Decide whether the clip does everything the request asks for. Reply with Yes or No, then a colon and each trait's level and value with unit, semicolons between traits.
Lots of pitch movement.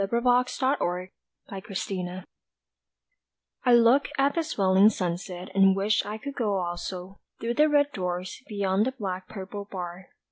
No: average, 4.3 semitones